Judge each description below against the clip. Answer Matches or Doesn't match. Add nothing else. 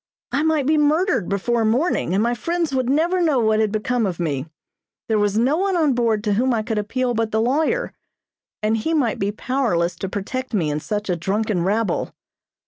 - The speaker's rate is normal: Doesn't match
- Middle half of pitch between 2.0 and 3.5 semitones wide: Doesn't match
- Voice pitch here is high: Matches